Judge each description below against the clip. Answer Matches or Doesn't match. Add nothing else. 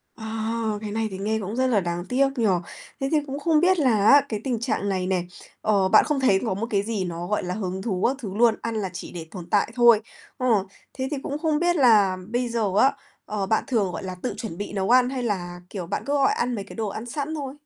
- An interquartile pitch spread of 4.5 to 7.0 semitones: Matches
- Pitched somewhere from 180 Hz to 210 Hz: Doesn't match